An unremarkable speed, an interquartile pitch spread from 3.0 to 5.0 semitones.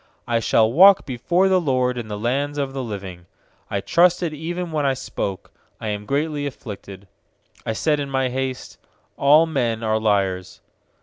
No: average, 170 wpm; wide, 5.5 semitones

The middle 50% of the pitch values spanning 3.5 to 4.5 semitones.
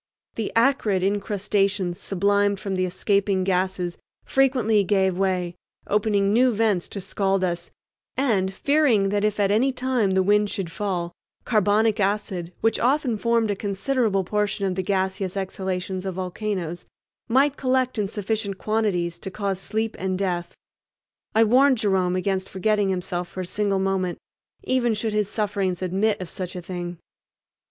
No: narrow, 2.5 semitones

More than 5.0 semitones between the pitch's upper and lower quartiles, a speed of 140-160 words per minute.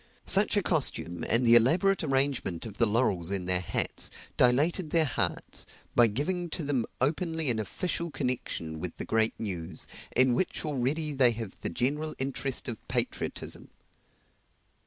Yes: wide, 5.5 semitones; average, 155 wpm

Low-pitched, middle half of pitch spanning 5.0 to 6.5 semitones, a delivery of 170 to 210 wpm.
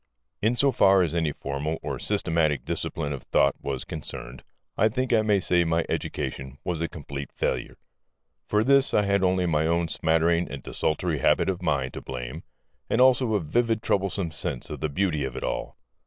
Yes: very low, 85 Hz; wide, 5.4 semitones; average, 190 wpm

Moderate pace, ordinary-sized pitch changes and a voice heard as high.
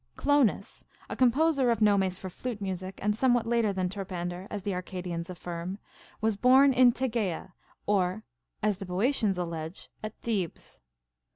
Yes: average, 155 wpm; average, 4.5 semitones; high, 200 Hz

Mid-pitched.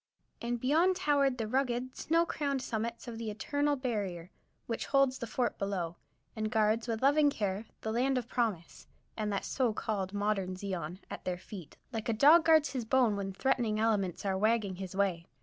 No: high, 225 Hz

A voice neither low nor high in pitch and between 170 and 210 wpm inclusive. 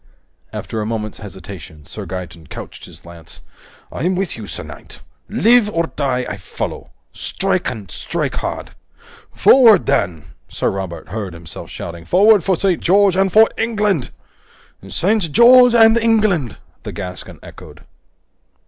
No: medium, 145 Hz; average, 140 wpm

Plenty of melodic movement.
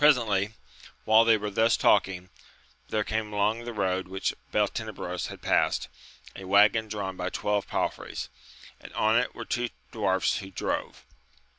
No: narrow, 2.6 semitones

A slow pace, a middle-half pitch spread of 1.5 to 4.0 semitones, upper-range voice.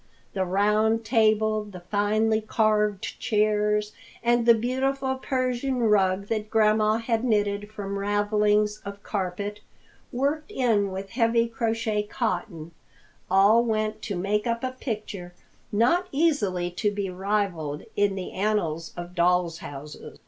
Yes: slow, 130 wpm; narrow, 2.5 semitones; high, 210 Hz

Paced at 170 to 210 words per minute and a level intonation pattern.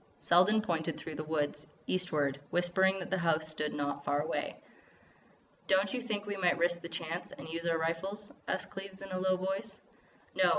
No: average, 195 wpm; average, 3.0 semitones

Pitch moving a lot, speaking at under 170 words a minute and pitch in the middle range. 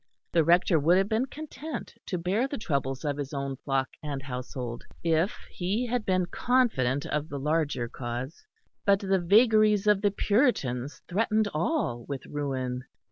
Yes: wide, 7.5 semitones; average, 160 wpm; medium, 165 Hz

